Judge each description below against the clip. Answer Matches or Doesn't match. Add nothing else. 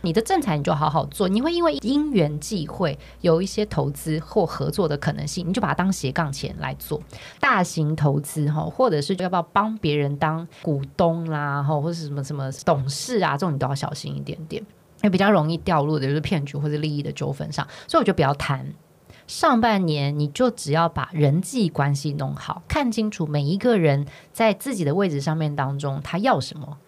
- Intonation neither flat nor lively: Matches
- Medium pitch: Matches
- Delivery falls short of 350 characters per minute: Matches